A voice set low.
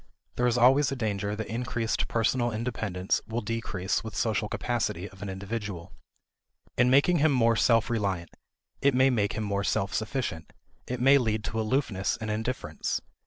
Yes: low, 115 Hz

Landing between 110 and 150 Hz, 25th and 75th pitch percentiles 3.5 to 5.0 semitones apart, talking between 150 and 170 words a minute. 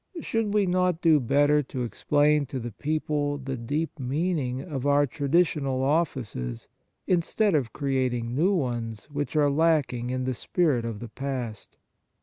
Yes: medium, 140 Hz; average, 3.9 semitones; average, 155 wpm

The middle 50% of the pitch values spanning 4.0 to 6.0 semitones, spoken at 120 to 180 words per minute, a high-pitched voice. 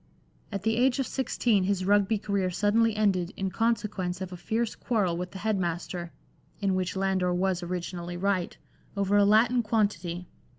No: average, 3.1 semitones; average, 170 wpm; high, 195 Hz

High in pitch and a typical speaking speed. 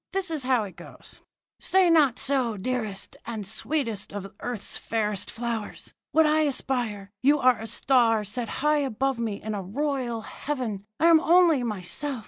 Yes: high, 245 Hz; average, 165 wpm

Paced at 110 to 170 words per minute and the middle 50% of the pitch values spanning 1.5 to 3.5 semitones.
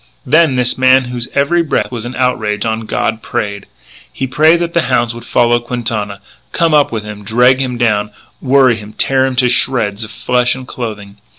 No: average, 195 wpm; average, 2.9 semitones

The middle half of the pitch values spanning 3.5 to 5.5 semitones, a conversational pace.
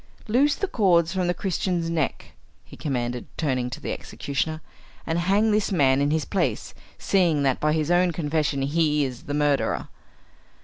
Yes: average, 4.2 semitones; average, 170 wpm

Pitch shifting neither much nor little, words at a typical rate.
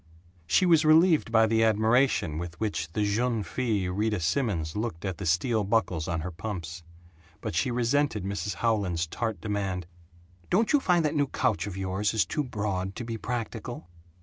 Yes: average, 4.6 semitones; average, 175 wpm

